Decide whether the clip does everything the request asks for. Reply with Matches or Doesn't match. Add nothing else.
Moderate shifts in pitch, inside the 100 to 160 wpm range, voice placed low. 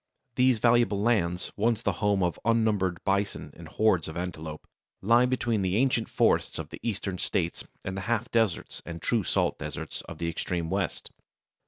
Doesn't match